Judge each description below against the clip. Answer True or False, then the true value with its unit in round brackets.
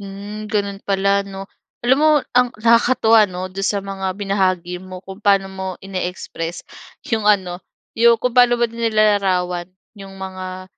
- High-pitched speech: True (195 Hz)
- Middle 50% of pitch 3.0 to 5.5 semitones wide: False (2.4 semitones)